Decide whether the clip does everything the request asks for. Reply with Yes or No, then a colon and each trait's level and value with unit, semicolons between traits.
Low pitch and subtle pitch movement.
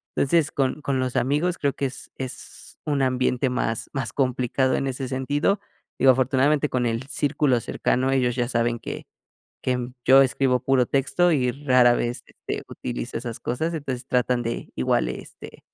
Yes: low, 130 Hz; narrow, 2.0 semitones